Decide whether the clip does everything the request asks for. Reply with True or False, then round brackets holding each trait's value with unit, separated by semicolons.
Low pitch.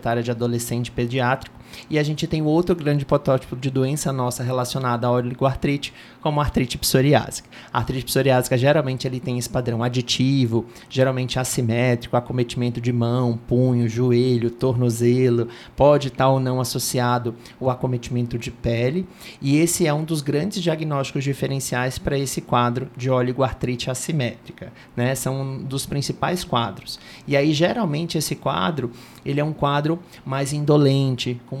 True (130 Hz)